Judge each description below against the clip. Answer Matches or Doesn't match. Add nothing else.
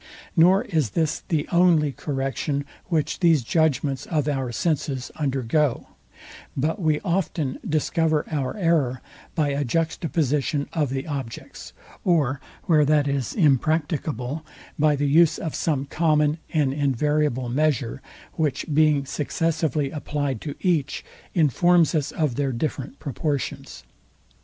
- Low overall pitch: Doesn't match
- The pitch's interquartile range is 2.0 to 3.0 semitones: Matches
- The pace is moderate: Doesn't match